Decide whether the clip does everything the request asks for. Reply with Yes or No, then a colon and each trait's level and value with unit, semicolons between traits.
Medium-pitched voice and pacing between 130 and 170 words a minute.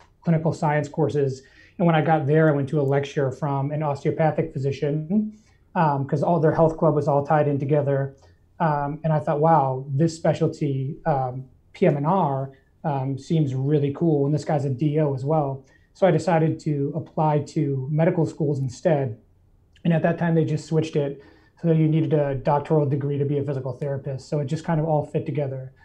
No: medium, 150 Hz; average, 195 wpm